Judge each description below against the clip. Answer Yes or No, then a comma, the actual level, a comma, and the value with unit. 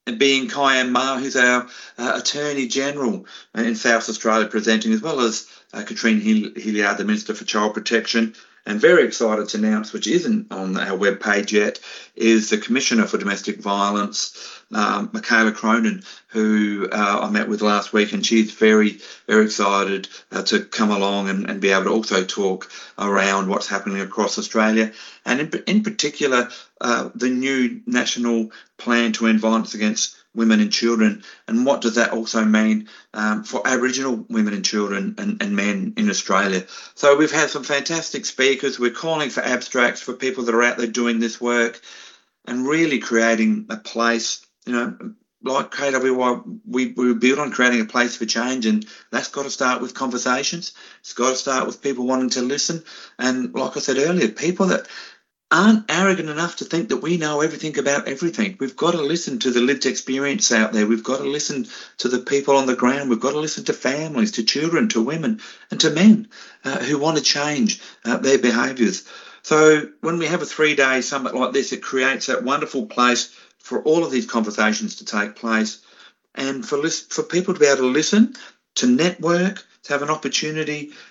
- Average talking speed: Yes, average, 190 wpm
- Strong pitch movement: Yes, wide, 5.8 semitones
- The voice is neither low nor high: No, low, 130 Hz